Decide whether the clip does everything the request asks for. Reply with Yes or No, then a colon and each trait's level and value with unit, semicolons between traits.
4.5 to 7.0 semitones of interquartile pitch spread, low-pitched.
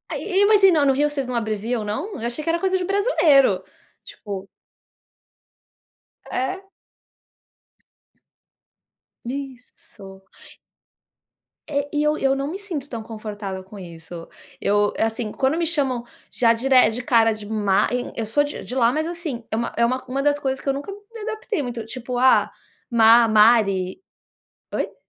No: average, 5.1 semitones; very high, 250 Hz